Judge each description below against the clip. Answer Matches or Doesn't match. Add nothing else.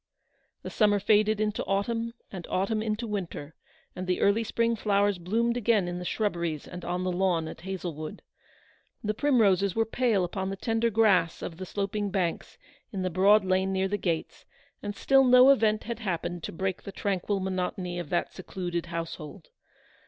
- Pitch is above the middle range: Matches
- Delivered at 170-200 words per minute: Matches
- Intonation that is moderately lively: Matches